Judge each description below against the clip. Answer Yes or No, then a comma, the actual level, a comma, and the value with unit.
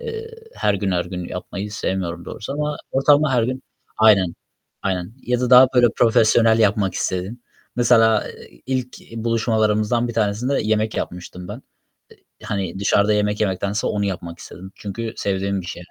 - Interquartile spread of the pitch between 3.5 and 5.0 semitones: Yes, average, 3.8 semitones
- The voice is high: No, low, 105 Hz